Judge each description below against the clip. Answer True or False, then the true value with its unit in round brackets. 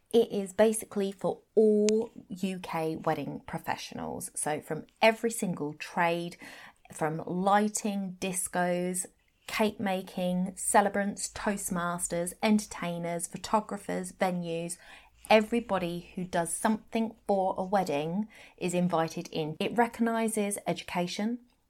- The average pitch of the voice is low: False (190 Hz)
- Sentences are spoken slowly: True (100 wpm)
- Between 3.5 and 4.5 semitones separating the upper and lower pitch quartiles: True (3.8 semitones)